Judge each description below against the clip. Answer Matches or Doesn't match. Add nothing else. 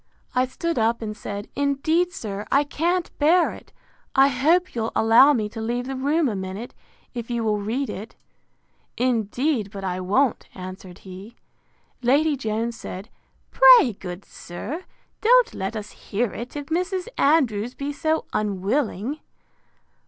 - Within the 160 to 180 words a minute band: Doesn't match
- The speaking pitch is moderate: Doesn't match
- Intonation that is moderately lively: Doesn't match